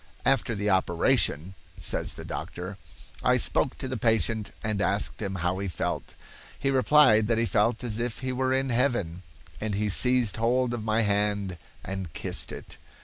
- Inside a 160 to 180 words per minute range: Yes, average, 175 wpm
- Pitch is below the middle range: Yes, low, 110 Hz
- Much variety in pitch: No, average, 3.8 semitones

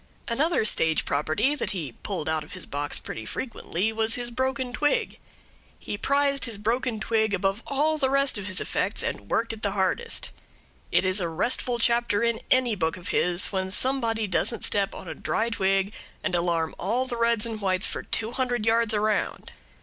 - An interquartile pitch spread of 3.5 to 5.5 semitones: Yes, average, 4.4 semitones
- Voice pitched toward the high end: Yes, high, 220 Hz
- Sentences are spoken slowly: No, average, 190 wpm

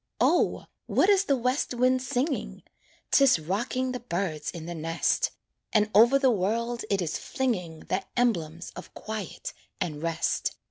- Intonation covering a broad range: Yes, wide, 6.9 semitones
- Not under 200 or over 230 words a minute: No, average, 150 wpm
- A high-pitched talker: Yes, high, 220 Hz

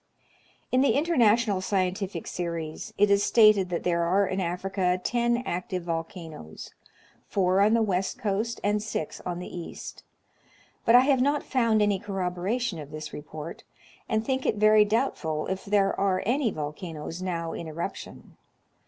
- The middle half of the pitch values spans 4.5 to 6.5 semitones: No, average, 4.0 semitones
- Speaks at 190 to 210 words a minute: No, average, 160 wpm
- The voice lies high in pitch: Yes, high, 195 Hz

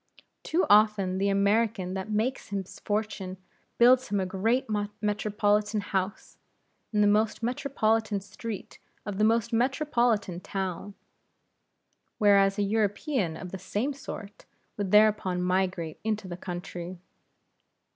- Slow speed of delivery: Yes, slow, 125 wpm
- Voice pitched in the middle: No, high, 205 Hz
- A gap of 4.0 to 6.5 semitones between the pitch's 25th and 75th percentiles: No, narrow, 2.6 semitones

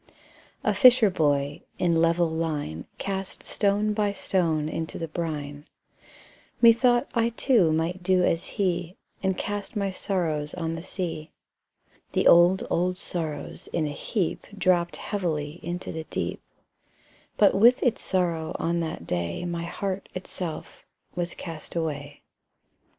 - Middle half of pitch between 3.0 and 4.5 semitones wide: Yes, average, 3.4 semitones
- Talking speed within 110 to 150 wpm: Yes, slow, 135 wpm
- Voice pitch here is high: No, medium, 175 Hz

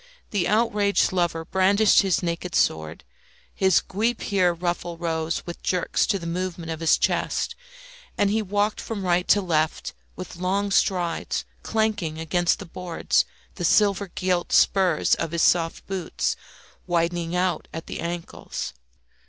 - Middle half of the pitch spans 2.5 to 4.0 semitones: Yes, average, 2.8 semitones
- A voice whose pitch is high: No, medium, 180 Hz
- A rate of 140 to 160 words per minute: Yes, average, 145 wpm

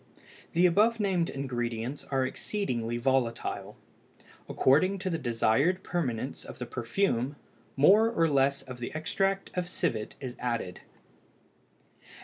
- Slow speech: Yes, slow, 125 wpm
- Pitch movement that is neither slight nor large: No, wide, 7.0 semitones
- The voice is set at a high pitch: No, low, 135 Hz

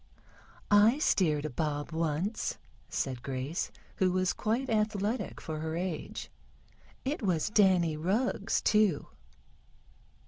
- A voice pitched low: No, medium, 185 Hz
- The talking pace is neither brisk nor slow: No, slow, 110 wpm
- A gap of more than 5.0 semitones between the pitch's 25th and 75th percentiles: Yes, wide, 5.5 semitones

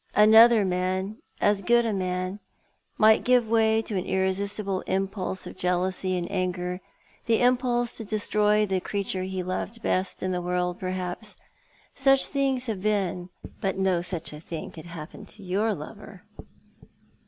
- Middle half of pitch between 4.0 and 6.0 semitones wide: No, average, 3.1 semitones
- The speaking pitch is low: No, high, 195 Hz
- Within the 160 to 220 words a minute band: Yes, average, 165 wpm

